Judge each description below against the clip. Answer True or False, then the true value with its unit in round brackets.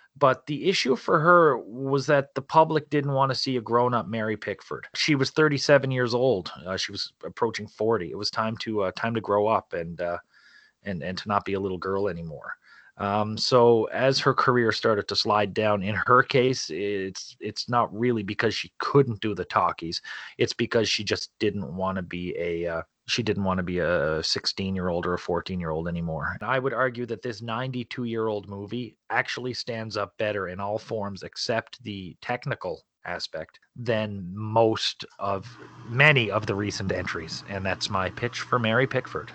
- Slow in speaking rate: False (200 wpm)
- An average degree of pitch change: True (4.1 semitones)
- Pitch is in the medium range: False (110 Hz)